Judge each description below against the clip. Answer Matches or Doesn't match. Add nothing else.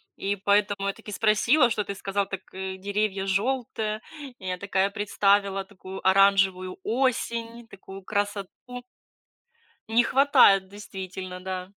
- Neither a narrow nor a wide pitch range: Doesn't match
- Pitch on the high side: Matches